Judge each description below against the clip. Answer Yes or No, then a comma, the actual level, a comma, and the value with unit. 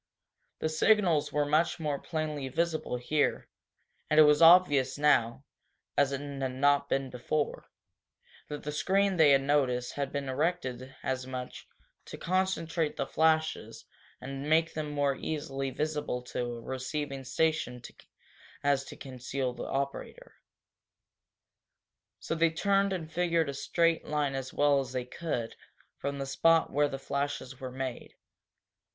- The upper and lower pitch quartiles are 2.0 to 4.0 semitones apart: Yes, average, 3.1 semitones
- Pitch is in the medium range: Yes, medium, 145 Hz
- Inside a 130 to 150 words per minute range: Yes, average, 145 wpm